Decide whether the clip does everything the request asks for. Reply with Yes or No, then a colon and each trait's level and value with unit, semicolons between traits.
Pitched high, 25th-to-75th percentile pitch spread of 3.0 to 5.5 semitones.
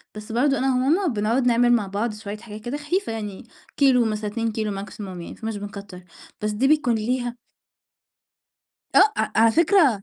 Yes: high, 230 Hz; average, 3.6 semitones